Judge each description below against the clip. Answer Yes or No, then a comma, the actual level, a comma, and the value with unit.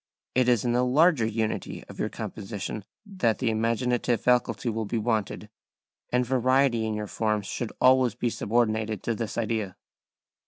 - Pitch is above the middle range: No, low, 115 Hz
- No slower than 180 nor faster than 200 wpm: No, average, 160 wpm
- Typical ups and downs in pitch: No, narrow, 2.3 semitones